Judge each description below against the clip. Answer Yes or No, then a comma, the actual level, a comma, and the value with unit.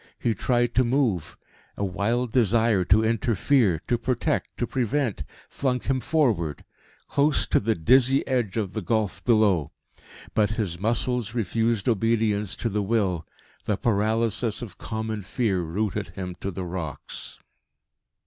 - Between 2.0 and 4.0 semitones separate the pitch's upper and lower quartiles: Yes, average, 3.6 semitones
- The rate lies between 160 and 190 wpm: No, average, 140 wpm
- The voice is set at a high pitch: No, low, 110 Hz